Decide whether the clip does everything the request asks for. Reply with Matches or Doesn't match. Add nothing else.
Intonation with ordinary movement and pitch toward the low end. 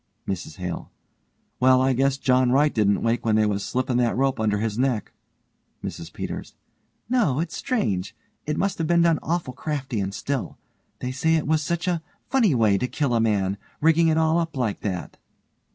Doesn't match